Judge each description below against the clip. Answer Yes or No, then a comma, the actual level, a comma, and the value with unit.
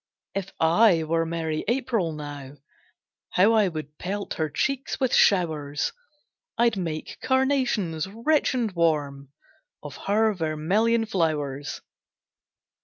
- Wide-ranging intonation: Yes, wide, 6.3 semitones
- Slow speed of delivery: Yes, slow, 110 wpm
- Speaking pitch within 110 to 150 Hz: No, medium, 175 Hz